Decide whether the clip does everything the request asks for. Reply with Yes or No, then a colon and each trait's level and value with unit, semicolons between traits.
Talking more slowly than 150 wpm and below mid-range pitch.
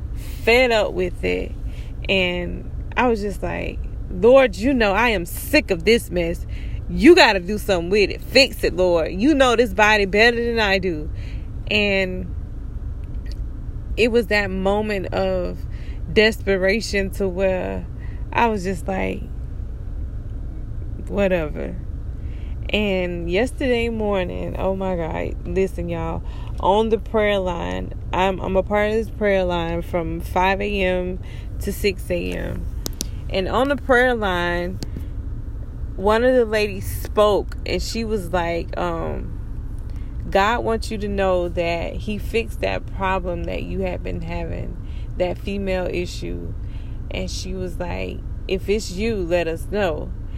No: average, 140 wpm; medium, 175 Hz